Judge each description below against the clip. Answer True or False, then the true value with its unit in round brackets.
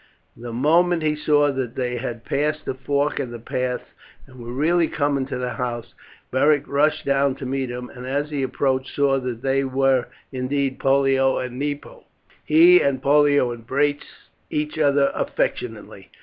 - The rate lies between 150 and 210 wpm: True (165 wpm)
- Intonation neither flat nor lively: False (2.3 semitones)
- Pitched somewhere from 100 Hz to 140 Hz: True (135 Hz)